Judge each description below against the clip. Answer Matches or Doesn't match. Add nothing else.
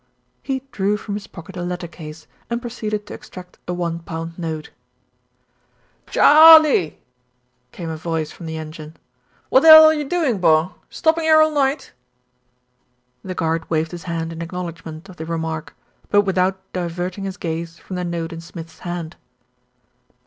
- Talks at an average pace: Matches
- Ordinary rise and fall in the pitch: Matches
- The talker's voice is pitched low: Doesn't match